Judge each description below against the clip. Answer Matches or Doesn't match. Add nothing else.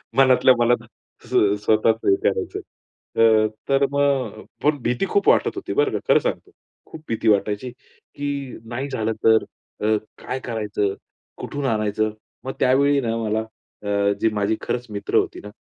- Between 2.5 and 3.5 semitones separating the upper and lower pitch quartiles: Doesn't match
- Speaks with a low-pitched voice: Matches